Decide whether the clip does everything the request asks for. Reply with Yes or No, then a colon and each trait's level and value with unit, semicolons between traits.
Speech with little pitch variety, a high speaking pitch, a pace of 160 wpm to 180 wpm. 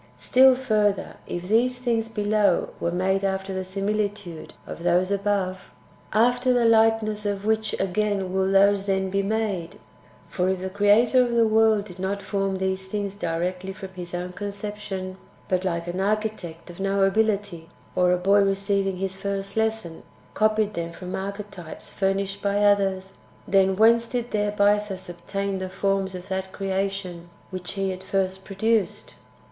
Yes: narrow, 1.9 semitones; high, 195 Hz; average, 170 wpm